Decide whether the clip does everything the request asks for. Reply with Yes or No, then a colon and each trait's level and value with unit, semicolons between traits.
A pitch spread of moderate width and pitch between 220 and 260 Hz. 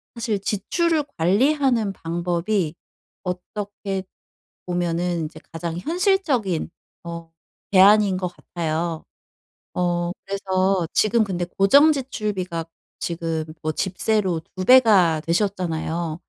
No: average, 3.8 semitones; medium, 185 Hz